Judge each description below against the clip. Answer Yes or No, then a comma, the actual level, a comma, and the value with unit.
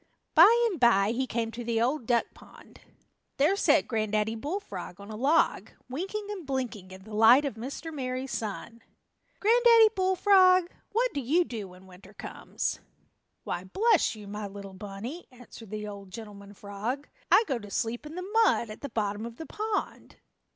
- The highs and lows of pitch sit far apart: Yes, wide, 8.0 semitones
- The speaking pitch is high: Yes, high, 235 Hz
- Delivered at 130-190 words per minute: Yes, average, 175 wpm